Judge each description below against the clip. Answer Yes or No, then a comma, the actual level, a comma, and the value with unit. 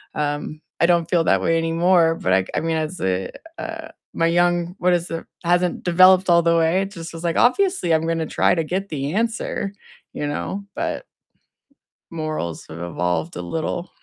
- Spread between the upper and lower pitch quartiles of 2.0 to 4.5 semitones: Yes, narrow, 2.6 semitones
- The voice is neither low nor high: Yes, medium, 165 Hz